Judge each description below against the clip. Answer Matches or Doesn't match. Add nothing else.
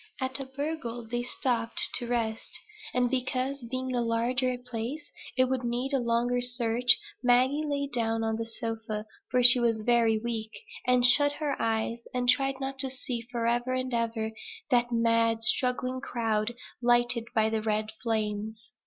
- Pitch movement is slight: Matches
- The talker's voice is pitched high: Matches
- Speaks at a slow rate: Doesn't match